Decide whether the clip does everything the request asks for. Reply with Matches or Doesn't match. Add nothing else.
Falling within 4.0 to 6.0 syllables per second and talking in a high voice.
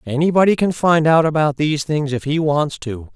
Doesn't match